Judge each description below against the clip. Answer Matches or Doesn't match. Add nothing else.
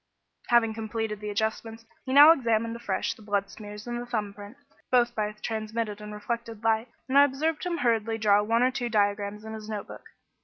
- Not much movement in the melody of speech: Matches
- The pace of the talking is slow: Doesn't match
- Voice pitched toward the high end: Matches